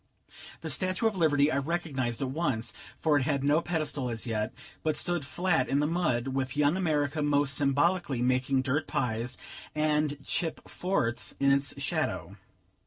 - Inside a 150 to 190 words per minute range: Yes, average, 165 wpm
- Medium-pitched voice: Yes, medium, 145 Hz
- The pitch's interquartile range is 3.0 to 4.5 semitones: Yes, average, 3.4 semitones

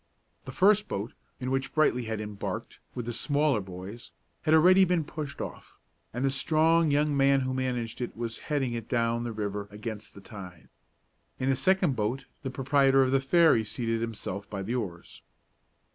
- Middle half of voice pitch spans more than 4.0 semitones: Yes, average, 4.4 semitones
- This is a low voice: Yes, low, 125 Hz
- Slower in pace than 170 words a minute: No, average, 180 wpm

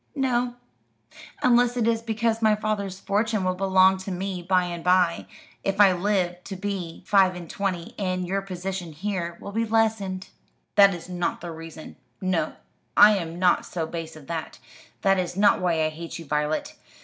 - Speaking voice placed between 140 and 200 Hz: Yes, medium, 185 Hz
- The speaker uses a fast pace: No, average, 180 wpm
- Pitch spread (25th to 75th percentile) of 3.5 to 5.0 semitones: No, average, 2.8 semitones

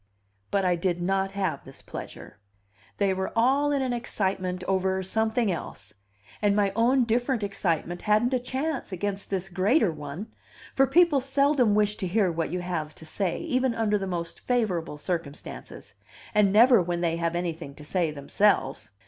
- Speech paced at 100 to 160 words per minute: No, average, 170 wpm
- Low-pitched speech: No, high, 195 Hz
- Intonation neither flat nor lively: Yes, average, 4.8 semitones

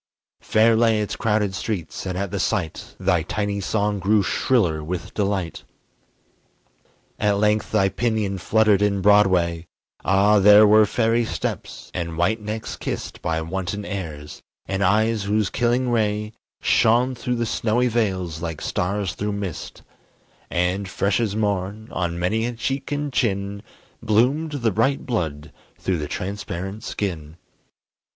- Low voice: Yes, low, 105 Hz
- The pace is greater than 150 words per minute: No, average, 145 wpm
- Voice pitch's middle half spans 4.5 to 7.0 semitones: No, average, 3.1 semitones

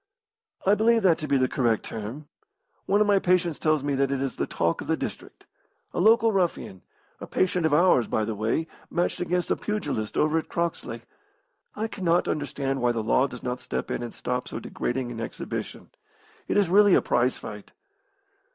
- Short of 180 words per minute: No, average, 195 wpm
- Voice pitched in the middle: Yes, medium, 145 Hz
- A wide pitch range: Yes, wide, 6.8 semitones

